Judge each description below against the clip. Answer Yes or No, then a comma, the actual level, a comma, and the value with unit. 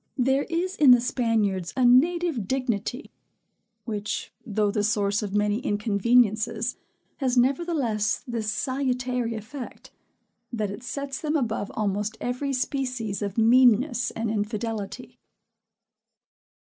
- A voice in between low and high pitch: No, high, 235 Hz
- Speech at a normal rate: No, slow, 115 wpm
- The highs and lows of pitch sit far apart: No, average, 3.7 semitones